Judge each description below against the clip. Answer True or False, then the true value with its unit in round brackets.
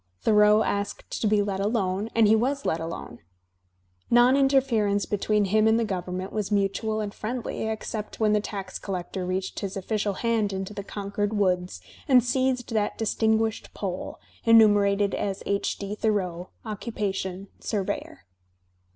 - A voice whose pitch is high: True (205 Hz)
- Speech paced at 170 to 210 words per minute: False (150 wpm)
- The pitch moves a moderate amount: False (2.1 semitones)